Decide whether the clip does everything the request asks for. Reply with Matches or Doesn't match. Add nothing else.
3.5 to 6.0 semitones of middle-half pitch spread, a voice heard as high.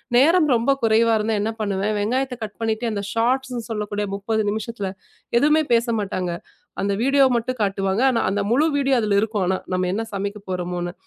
Doesn't match